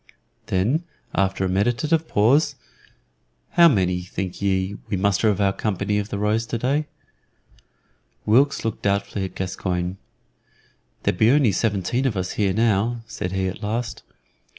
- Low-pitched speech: Yes, low, 105 Hz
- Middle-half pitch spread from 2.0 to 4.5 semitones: Yes, average, 3.7 semitones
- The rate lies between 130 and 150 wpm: Yes, average, 145 wpm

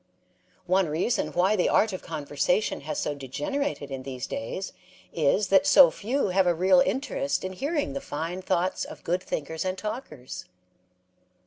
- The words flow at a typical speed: Yes, average, 160 wpm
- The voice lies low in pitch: No, medium, 185 Hz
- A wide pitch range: Yes, wide, 5.9 semitones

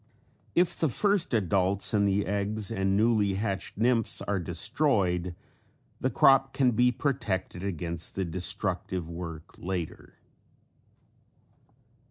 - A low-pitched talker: Yes, low, 100 Hz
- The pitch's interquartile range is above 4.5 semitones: No, average, 4.1 semitones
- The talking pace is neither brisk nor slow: No, slow, 115 wpm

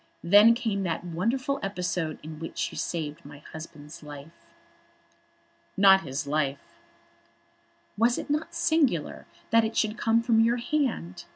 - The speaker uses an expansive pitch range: Yes, wide, 6.9 semitones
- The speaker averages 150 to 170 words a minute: No, slow, 135 wpm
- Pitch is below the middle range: No, high, 190 Hz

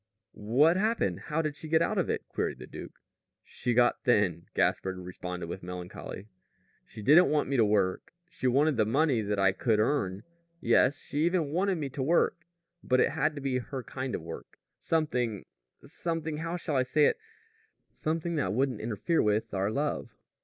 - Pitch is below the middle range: Yes, low, 130 Hz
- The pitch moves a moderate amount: No, wide, 6.8 semitones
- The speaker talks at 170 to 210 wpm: Yes, average, 185 wpm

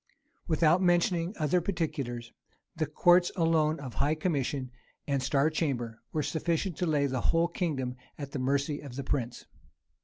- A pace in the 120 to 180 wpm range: Yes, average, 155 wpm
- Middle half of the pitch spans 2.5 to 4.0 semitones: Yes, average, 3.7 semitones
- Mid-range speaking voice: Yes, medium, 150 Hz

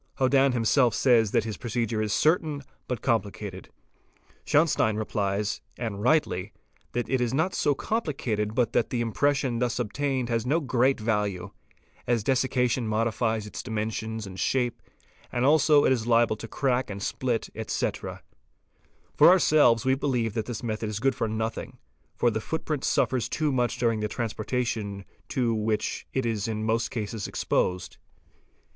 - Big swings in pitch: No, average, 3.3 semitones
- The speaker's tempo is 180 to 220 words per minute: No, average, 160 wpm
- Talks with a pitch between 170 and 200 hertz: No, low, 115 Hz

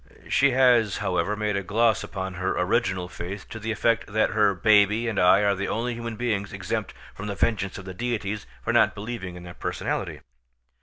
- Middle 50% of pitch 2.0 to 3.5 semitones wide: Yes, average, 3.1 semitones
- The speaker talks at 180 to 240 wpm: Yes, average, 200 wpm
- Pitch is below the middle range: Yes, low, 105 Hz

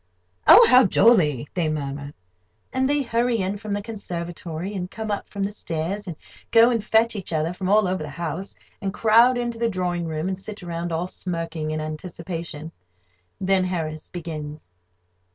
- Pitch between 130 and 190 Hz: Yes, medium, 185 Hz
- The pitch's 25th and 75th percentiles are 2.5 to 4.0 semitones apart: No, average, 4.6 semitones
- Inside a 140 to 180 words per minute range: Yes, average, 175 wpm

